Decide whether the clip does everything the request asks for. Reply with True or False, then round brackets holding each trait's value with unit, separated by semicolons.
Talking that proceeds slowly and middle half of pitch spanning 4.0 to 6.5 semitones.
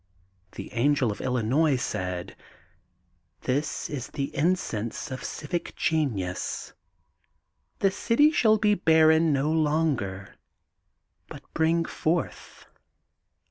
True (100 wpm; 5.2 semitones)